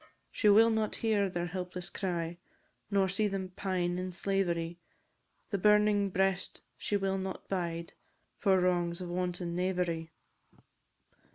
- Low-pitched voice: No, medium, 185 Hz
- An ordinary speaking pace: No, slow, 130 wpm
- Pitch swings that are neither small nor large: No, narrow, 2.0 semitones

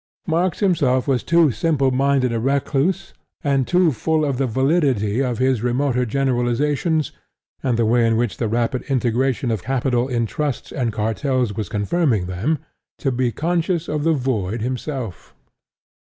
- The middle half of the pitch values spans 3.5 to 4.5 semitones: Yes, average, 3.9 semitones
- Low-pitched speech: Yes, low, 130 Hz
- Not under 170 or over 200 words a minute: No, average, 150 wpm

